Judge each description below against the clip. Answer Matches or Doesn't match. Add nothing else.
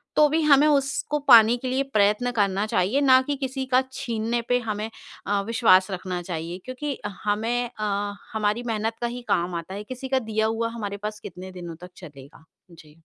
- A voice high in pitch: Matches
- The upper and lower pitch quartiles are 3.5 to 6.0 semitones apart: Matches